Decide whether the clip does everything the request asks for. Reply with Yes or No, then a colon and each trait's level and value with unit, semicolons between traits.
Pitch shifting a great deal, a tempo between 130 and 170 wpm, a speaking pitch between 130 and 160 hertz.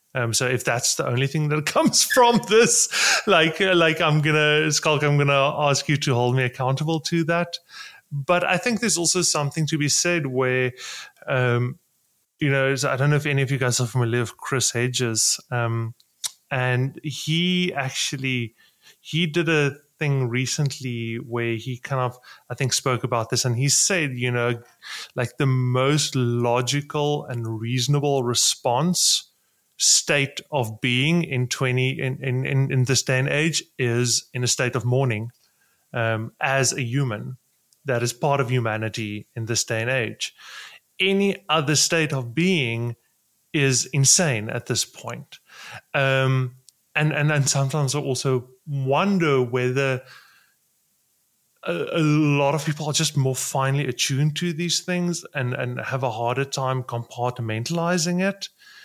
No: average, 3.5 semitones; average, 160 wpm; low, 135 Hz